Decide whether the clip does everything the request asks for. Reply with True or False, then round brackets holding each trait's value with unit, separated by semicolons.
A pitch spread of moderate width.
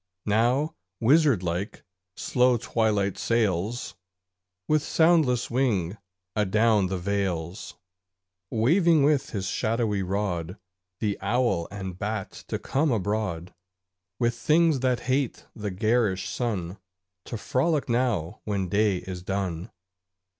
True (4.7 semitones)